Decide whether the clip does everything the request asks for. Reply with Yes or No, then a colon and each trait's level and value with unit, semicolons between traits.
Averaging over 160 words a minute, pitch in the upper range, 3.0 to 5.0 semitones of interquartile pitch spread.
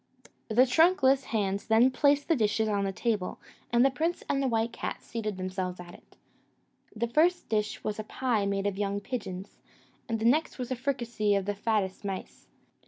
Yes: average, 185 wpm; high, 220 Hz; average, 4.3 semitones